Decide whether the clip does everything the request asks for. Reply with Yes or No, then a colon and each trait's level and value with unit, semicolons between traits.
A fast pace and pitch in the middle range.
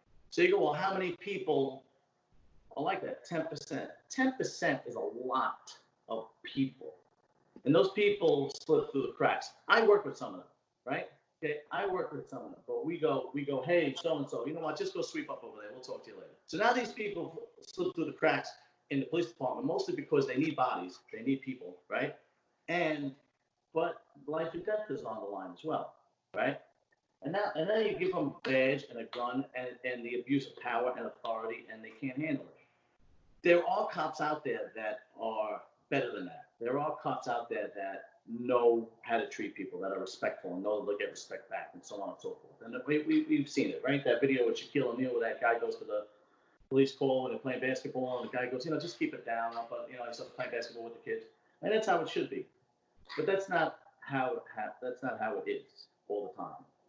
Yes: fast, 230 wpm; medium, 160 Hz